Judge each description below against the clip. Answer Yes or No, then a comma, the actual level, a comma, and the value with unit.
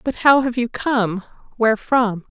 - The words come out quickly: No, average, 180 wpm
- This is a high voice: Yes, high, 235 Hz